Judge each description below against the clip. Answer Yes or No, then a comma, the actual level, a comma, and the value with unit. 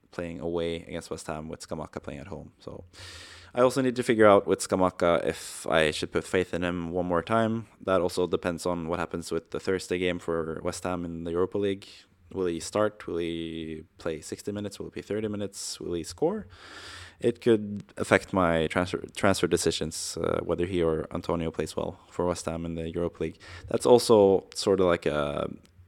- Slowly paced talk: No, fast, 205 wpm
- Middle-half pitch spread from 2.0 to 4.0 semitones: Yes, average, 2.7 semitones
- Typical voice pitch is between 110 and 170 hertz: No, very low, 90 Hz